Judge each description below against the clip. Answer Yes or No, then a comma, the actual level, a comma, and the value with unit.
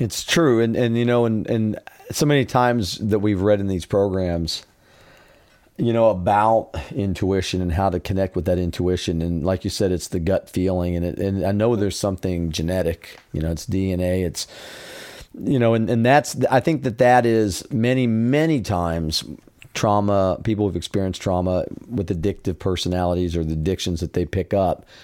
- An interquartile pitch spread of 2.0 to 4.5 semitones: Yes, average, 4.1 semitones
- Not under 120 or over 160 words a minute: No, average, 185 wpm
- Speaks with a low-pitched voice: Yes, very low, 95 Hz